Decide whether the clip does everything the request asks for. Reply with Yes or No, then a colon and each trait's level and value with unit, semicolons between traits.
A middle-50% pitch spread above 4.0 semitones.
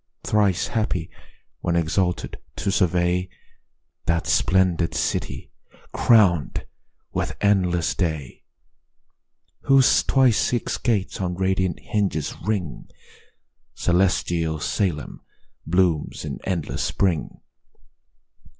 No: average, 2.8 semitones